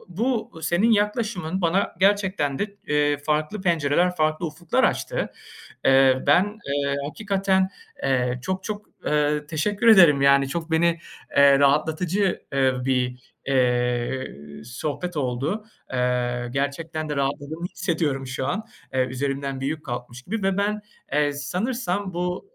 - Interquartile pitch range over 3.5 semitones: Yes, wide, 5.5 semitones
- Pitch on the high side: No, medium, 155 Hz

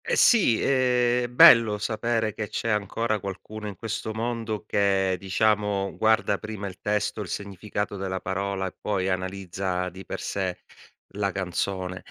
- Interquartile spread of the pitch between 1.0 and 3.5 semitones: Yes, narrow, 2.4 semitones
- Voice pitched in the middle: No, low, 100 Hz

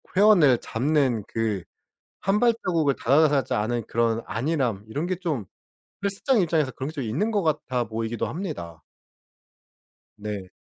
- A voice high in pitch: No, low, 135 Hz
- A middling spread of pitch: No, wide, 6.8 semitones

